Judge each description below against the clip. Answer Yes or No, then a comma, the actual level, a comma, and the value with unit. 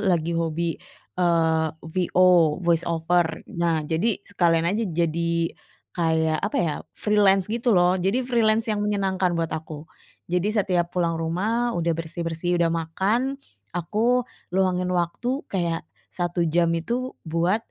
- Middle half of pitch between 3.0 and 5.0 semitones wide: Yes, average, 3.3 semitones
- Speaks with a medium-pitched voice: Yes, medium, 175 Hz